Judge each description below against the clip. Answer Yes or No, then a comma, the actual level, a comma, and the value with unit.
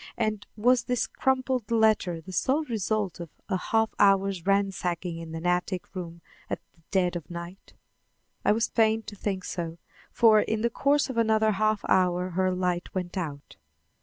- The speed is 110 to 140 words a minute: No, average, 170 wpm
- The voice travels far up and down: No, average, 3.7 semitones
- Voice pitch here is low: No, high, 195 Hz